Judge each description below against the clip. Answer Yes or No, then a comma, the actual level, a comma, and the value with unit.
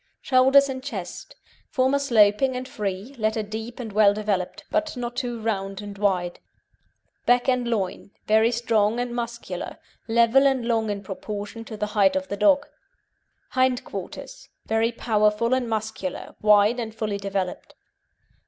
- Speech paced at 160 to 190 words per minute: No, average, 150 wpm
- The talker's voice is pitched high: Yes, high, 225 Hz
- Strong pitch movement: No, average, 3.1 semitones